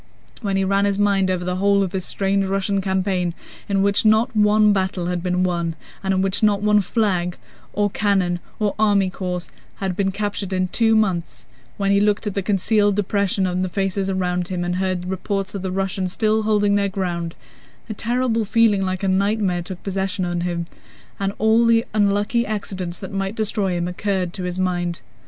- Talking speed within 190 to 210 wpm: Yes, average, 195 wpm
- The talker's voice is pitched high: Yes, high, 195 Hz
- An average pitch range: No, narrow, 2.0 semitones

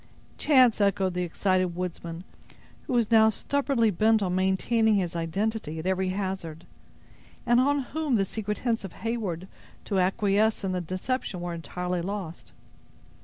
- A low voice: No, high, 195 Hz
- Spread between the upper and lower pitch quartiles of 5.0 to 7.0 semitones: No, average, 3.7 semitones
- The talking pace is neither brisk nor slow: Yes, average, 150 wpm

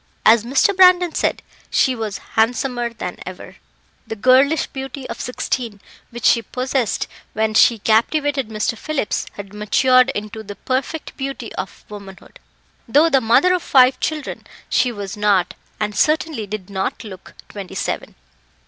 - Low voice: No, high, 235 Hz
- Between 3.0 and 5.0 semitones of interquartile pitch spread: Yes, average, 4.3 semitones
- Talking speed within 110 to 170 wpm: Yes, average, 150 wpm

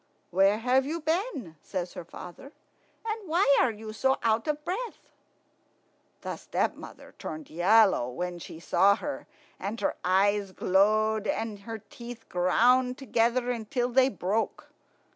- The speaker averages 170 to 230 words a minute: No, average, 140 wpm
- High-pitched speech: Yes, high, 225 Hz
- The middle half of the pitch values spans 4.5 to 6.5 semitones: Yes, average, 5.2 semitones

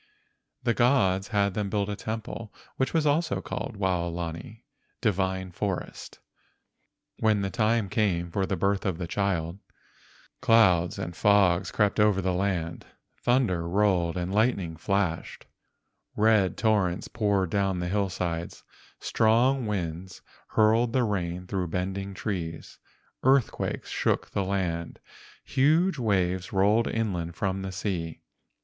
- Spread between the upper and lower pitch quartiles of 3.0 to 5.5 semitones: Yes, average, 3.4 semitones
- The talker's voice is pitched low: Yes, low, 100 Hz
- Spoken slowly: Yes, slow, 130 wpm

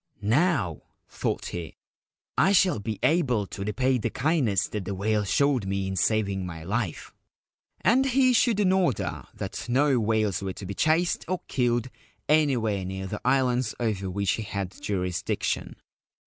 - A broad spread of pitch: Yes, wide, 6.5 semitones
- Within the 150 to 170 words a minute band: Yes, average, 165 wpm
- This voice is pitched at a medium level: No, low, 110 Hz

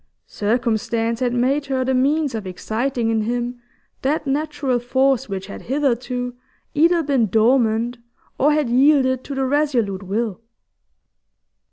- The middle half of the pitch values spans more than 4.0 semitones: No, average, 3.3 semitones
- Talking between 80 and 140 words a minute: Yes, slow, 135 wpm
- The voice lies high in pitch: Yes, very high, 250 Hz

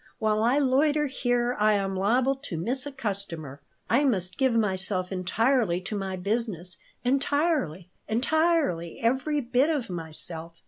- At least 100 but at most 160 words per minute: Yes, average, 140 wpm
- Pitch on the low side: No, high, 225 Hz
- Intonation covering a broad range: Yes, wide, 6.5 semitones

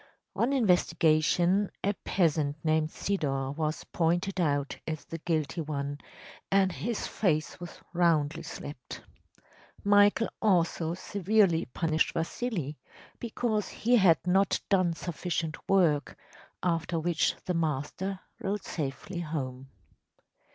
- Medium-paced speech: No, slow, 115 wpm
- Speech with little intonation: No, average, 4.0 semitones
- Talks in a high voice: No, medium, 170 Hz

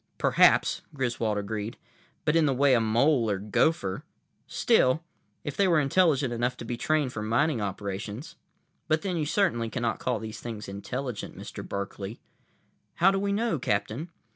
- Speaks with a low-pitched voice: Yes, low, 125 Hz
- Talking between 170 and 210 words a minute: No, average, 155 wpm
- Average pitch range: No, wide, 6.2 semitones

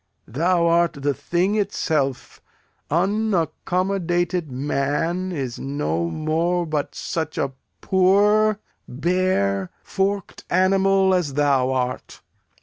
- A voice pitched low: No, medium, 170 Hz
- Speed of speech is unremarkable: No, slow, 95 wpm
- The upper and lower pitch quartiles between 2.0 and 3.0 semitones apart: No, average, 4.9 semitones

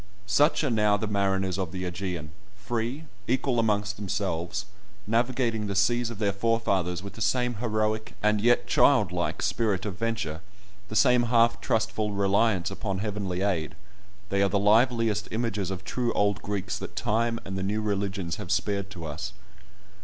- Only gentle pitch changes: No, average, 3.0 semitones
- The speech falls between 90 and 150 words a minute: No, average, 170 wpm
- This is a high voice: No, low, 105 Hz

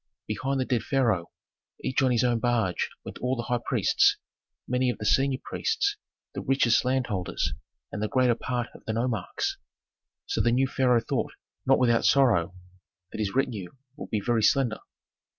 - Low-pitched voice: Yes, low, 120 Hz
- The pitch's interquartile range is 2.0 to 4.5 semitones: Yes, average, 2.9 semitones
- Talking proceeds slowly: No, average, 170 wpm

